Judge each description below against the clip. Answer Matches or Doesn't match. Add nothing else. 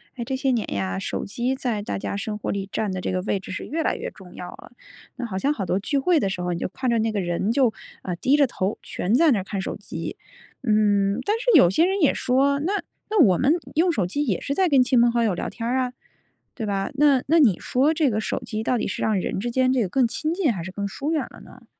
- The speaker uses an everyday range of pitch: Doesn't match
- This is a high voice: Matches